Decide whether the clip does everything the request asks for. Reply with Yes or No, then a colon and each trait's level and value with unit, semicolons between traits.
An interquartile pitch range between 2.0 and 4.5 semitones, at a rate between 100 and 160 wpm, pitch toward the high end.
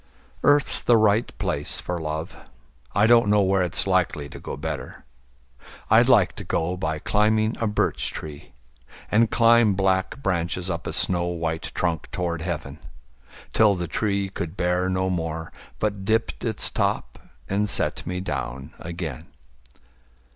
No: average, 4.2 semitones; average, 150 wpm; very low, 90 Hz